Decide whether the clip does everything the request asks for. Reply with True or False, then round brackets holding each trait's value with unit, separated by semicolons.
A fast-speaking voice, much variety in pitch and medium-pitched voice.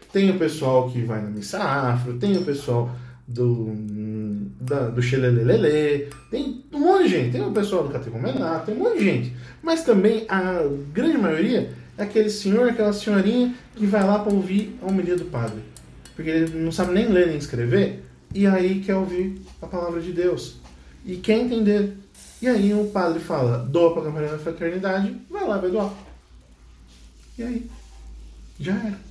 False (175 wpm; 8.8 semitones; 170 Hz)